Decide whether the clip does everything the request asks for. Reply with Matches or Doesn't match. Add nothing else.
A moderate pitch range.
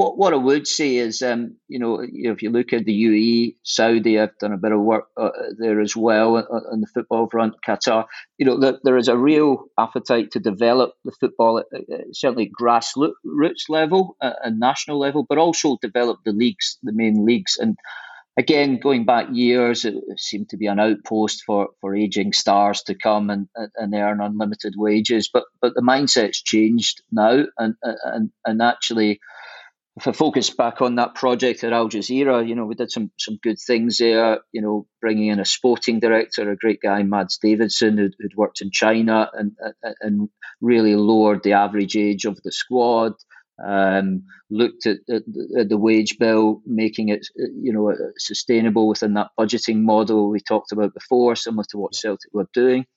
Doesn't match